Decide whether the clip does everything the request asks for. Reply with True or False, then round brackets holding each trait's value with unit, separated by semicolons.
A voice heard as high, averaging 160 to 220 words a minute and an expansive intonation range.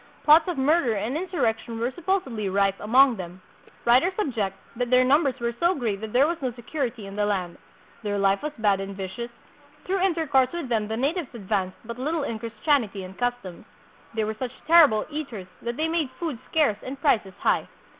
True (240 Hz; 200 wpm; 6.1 semitones)